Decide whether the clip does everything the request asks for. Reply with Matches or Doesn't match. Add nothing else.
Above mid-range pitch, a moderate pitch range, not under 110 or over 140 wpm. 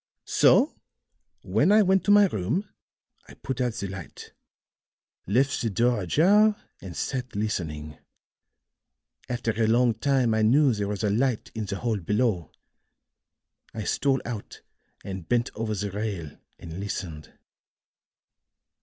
Doesn't match